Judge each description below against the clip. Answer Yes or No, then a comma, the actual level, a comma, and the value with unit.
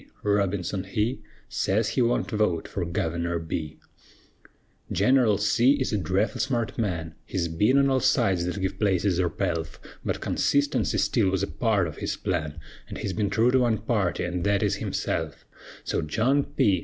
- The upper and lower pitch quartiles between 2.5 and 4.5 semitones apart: No, average, 5.0 semitones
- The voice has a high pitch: No, low, 100 Hz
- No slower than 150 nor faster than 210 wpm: Yes, average, 170 wpm